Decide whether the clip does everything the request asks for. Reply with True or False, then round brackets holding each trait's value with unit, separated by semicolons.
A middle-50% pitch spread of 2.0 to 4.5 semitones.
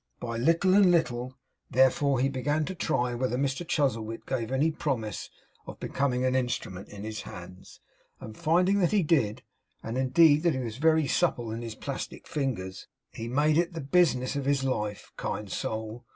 False (5.1 semitones)